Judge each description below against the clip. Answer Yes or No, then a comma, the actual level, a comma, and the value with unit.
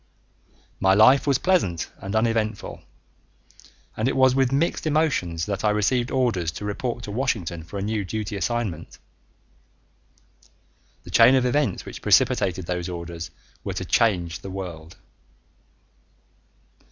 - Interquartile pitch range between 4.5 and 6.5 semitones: Yes, wide, 5.6 semitones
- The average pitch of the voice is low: Yes, low, 105 Hz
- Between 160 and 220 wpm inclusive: No, slow, 135 wpm